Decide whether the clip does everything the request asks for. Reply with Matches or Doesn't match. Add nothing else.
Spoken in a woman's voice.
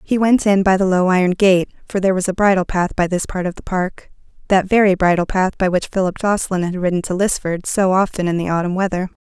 Matches